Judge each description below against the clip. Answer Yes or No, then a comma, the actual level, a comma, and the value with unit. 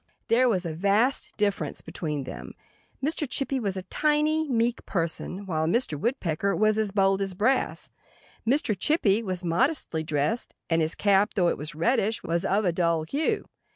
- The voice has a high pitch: Yes, high, 200 Hz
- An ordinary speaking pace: Yes, average, 170 wpm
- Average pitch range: No, wide, 6.0 semitones